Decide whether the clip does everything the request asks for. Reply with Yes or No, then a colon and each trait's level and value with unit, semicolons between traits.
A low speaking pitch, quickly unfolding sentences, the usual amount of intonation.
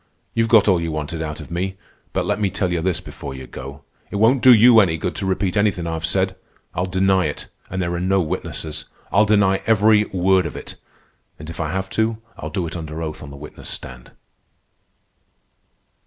Yes: very low, 95 Hz; fast, 210 wpm; average, 3.7 semitones